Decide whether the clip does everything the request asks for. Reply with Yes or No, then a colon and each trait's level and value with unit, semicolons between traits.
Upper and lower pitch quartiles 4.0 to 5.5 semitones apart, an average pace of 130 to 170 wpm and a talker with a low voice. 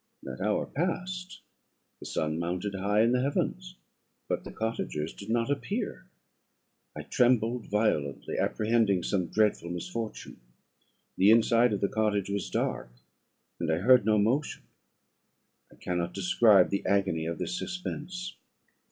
Yes: average, 5.1 semitones; slow, 135 wpm; low, 105 Hz